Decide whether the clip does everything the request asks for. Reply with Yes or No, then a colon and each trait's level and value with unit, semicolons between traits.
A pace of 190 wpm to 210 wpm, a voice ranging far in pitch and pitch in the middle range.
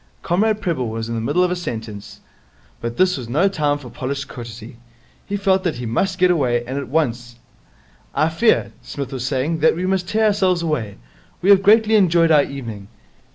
Yes: average, 200 wpm; wide, 7.3 semitones; medium, 150 Hz